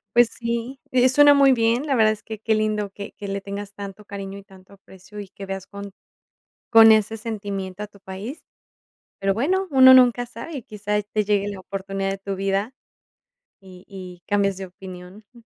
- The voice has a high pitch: Yes, high, 205 Hz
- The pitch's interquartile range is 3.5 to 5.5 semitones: No, average, 2.8 semitones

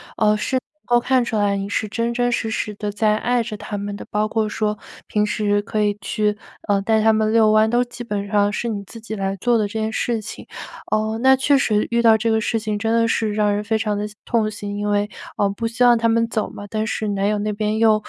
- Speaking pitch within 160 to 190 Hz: No, high, 215 Hz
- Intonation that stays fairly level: Yes, narrow, 1.7 semitones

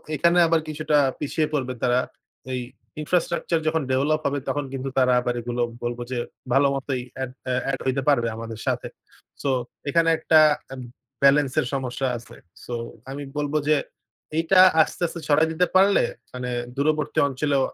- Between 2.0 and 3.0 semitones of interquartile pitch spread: No, average, 3.4 semitones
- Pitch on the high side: No, medium, 140 Hz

